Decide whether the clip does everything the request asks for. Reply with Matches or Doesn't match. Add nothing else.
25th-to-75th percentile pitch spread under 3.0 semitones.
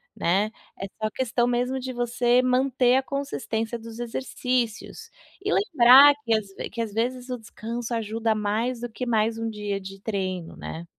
Matches